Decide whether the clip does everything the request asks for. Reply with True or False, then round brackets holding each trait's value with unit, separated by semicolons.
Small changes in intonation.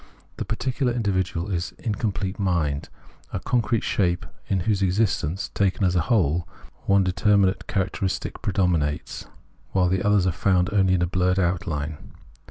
True (2.2 semitones)